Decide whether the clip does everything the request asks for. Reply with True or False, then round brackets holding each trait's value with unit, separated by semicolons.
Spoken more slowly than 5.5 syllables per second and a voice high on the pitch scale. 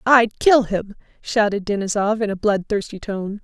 True (4.6 syllables/s; 210 Hz)